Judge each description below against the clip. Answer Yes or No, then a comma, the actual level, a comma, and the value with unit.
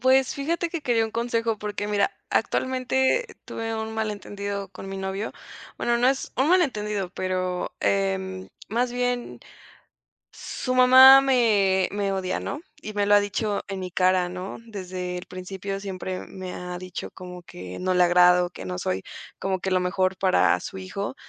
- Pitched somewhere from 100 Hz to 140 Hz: No, high, 200 Hz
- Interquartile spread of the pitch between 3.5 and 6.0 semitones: Yes, average, 4.0 semitones